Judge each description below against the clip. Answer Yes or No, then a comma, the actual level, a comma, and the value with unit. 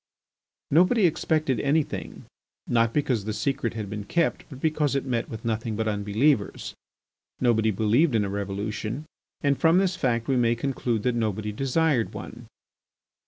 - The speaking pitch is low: Yes, low, 120 Hz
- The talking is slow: No, average, 155 wpm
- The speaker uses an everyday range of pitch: Yes, average, 4.9 semitones